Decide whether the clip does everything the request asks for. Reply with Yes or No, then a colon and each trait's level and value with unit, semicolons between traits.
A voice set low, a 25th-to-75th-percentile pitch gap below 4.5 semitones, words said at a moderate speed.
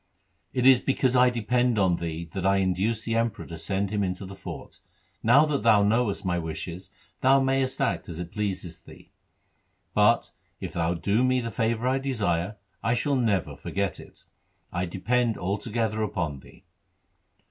No: low, 105 Hz; average, 5.0 semitones; average, 170 wpm